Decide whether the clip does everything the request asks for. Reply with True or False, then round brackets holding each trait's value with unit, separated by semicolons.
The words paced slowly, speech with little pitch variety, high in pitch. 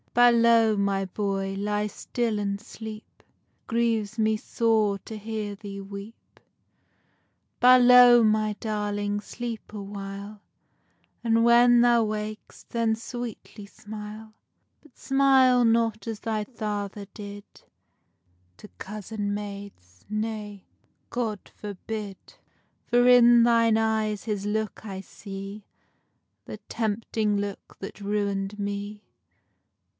True (110 wpm; 2.1 semitones; 215 Hz)